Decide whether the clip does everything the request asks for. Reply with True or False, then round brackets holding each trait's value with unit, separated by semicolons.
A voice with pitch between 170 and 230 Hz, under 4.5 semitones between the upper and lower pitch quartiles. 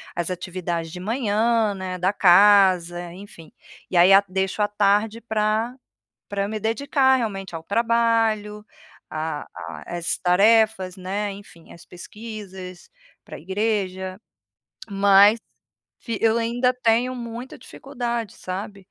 True (205 Hz; 3.4 semitones)